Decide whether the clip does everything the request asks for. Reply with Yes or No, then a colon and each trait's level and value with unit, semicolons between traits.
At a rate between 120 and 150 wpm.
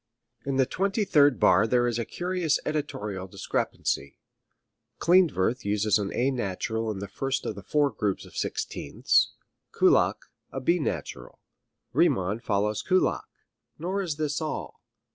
Yes: average, 140 wpm